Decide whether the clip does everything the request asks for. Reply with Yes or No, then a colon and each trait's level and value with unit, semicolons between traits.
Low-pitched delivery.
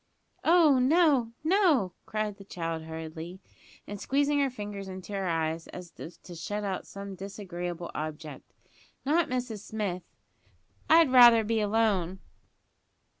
No: high, 205 Hz